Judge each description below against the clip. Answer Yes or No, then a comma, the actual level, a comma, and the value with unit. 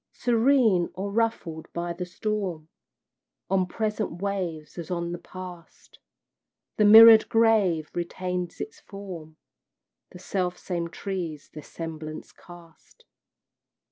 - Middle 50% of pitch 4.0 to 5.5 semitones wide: No, average, 3.4 semitones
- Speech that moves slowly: Yes, slow, 110 wpm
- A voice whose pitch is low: No, medium, 180 Hz